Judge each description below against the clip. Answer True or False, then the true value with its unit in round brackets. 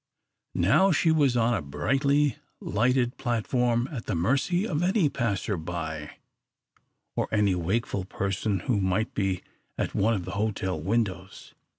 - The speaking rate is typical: True (145 wpm)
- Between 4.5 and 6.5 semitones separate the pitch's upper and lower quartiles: True (5.5 semitones)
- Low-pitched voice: True (110 Hz)